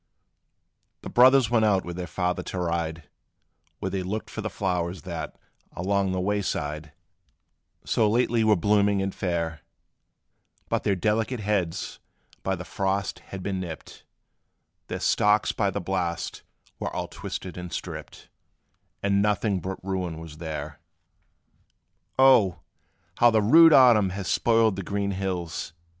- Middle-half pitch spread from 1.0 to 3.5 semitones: Yes, average, 3.2 semitones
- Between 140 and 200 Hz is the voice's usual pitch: No, very low, 95 Hz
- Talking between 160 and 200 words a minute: No, average, 145 wpm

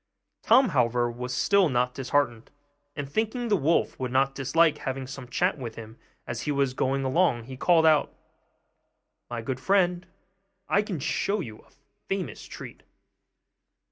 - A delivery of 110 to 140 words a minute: No, average, 155 wpm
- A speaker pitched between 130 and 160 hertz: Yes, low, 135 Hz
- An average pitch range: No, wide, 5.8 semitones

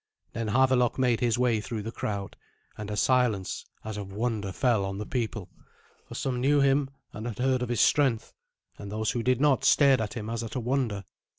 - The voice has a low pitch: Yes, low, 115 Hz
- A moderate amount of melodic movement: Yes, average, 3.2 semitones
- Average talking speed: No, fast, 210 wpm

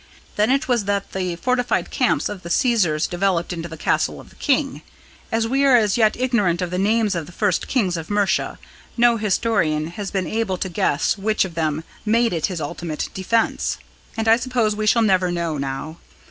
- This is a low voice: No, high, 200 Hz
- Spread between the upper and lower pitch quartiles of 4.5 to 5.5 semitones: Yes, average, 4.9 semitones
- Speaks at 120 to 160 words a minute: No, average, 200 wpm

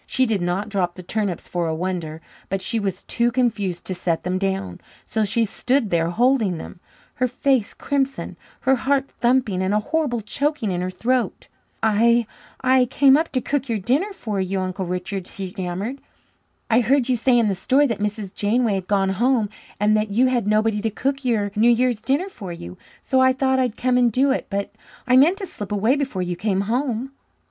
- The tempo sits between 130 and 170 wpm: No, fast, 205 wpm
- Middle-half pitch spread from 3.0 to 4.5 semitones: No, average, 5.0 semitones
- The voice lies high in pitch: Yes, high, 220 Hz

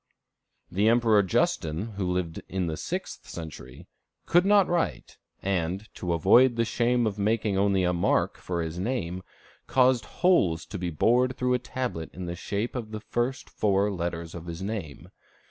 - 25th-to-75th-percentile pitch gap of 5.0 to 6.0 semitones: Yes, wide, 5.6 semitones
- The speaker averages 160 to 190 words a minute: Yes, average, 170 wpm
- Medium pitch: No, low, 100 Hz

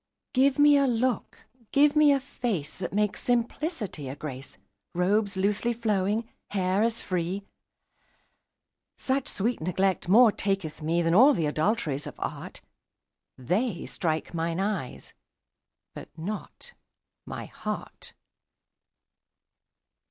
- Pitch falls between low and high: No, high, 200 Hz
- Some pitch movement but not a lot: No, wide, 5.9 semitones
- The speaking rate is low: Yes, slow, 120 wpm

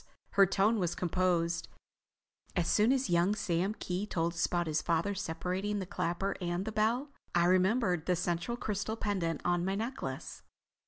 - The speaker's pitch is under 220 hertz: Yes, medium, 185 Hz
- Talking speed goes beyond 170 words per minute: No, average, 165 wpm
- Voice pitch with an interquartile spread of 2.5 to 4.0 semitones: Yes, average, 3.3 semitones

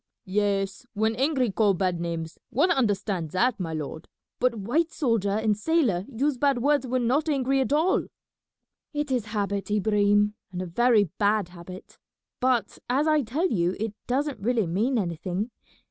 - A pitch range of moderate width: Yes, average, 5.0 semitones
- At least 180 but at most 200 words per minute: No, average, 160 wpm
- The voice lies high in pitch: Yes, high, 220 Hz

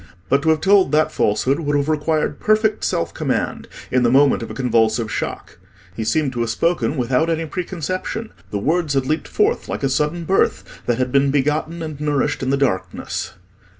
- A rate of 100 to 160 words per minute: No, average, 195 wpm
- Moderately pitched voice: Yes, medium, 145 Hz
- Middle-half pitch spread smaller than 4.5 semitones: Yes, average, 4.1 semitones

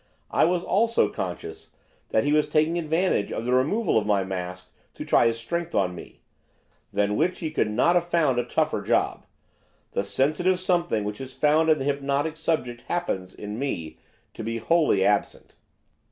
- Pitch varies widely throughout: Yes, wide, 8.1 semitones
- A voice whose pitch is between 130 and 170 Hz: Yes, medium, 140 Hz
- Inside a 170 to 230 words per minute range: Yes, average, 180 wpm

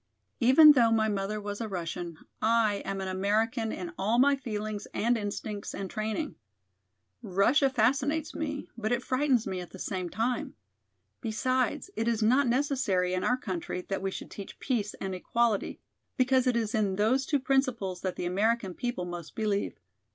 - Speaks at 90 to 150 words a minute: No, average, 175 wpm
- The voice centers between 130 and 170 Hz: No, high, 220 Hz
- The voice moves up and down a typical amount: Yes, average, 4.5 semitones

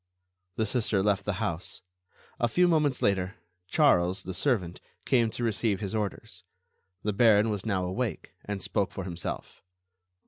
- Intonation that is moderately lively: Yes, average, 3.6 semitones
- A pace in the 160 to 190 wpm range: No, average, 150 wpm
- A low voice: Yes, low, 105 Hz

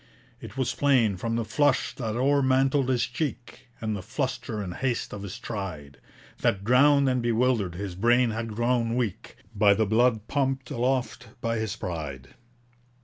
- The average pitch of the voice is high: No, low, 115 Hz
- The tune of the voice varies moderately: Yes, average, 3.9 semitones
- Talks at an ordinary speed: Yes, average, 160 wpm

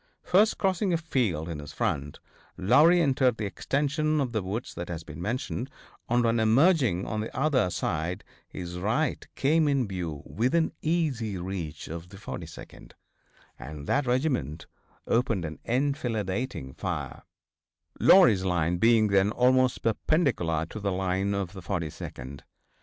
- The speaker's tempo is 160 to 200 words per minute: No, average, 145 wpm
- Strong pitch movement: Yes, wide, 7.3 semitones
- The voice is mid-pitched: No, low, 110 Hz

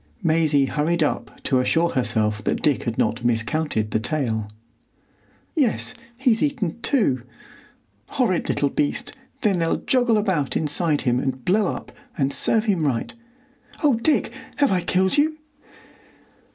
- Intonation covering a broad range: Yes, wide, 8.8 semitones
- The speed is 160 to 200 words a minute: No, average, 140 wpm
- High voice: No, medium, 160 Hz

